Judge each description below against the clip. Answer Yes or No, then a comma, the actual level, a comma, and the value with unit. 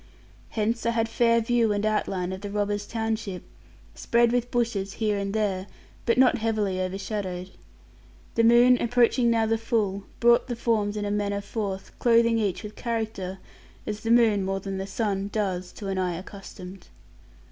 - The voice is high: Yes, high, 210 Hz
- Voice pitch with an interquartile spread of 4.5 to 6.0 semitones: No, average, 2.9 semitones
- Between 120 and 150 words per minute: No, average, 170 wpm